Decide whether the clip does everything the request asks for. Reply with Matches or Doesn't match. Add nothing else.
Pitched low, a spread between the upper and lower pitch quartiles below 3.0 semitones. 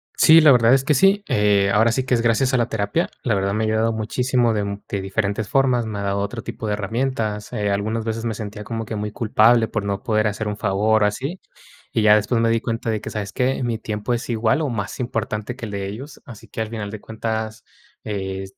Matches